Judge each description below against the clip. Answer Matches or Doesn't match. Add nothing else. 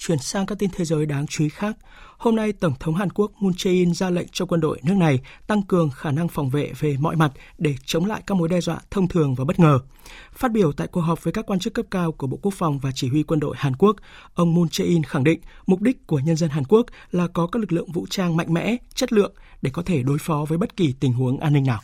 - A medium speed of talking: Doesn't match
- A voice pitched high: Doesn't match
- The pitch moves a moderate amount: Matches